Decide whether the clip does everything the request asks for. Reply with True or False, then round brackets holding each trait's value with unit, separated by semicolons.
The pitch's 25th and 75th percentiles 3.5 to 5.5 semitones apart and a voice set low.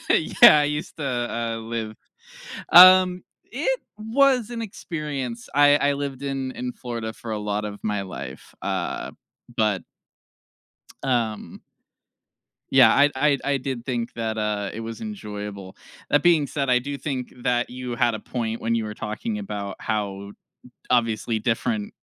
True (4.9 semitones; 125 Hz)